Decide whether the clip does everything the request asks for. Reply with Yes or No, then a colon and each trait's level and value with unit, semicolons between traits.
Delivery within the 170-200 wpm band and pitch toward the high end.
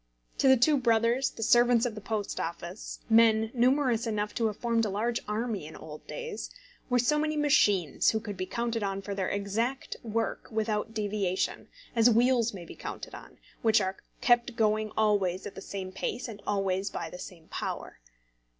Yes: average, 185 wpm; high, 220 Hz